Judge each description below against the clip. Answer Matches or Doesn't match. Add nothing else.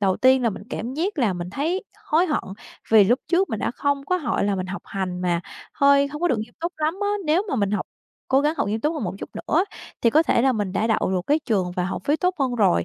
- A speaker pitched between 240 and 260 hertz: Matches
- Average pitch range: Doesn't match